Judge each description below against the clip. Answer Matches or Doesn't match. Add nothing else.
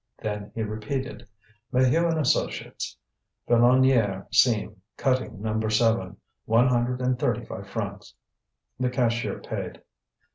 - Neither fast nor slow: Doesn't match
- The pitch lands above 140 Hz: Doesn't match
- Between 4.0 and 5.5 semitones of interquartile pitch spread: Doesn't match